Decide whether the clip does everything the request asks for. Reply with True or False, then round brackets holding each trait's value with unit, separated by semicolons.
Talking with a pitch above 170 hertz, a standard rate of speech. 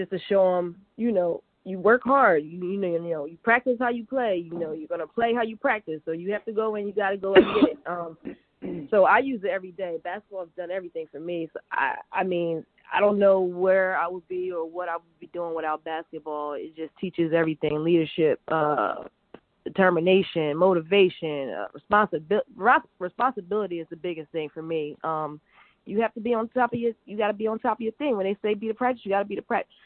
False (185 Hz; 235 wpm)